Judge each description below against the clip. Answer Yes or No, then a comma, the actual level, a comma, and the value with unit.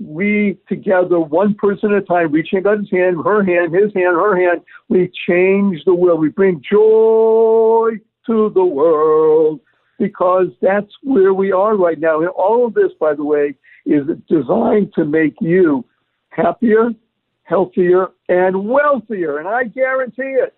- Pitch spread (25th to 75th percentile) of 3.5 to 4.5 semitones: Yes, average, 4.0 semitones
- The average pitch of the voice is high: Yes, high, 200 Hz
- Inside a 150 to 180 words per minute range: Yes, average, 155 wpm